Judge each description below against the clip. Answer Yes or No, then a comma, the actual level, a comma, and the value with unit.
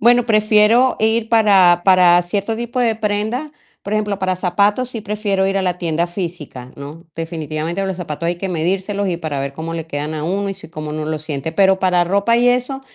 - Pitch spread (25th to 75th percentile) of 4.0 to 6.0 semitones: Yes, average, 4.4 semitones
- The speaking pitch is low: No, high, 190 Hz